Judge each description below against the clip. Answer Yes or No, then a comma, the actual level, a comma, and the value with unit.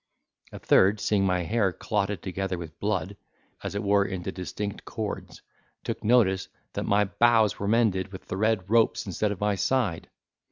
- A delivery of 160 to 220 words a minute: Yes, average, 170 wpm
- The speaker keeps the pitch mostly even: Yes, narrow, 2.3 semitones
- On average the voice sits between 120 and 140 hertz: No, low, 100 Hz